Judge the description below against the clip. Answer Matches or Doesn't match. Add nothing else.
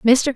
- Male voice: Doesn't match